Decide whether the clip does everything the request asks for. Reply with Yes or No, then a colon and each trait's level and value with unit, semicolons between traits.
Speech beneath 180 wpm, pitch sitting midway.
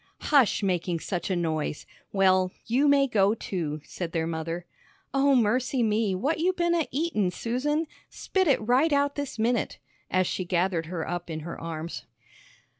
No: average, 170 wpm; high, 205 Hz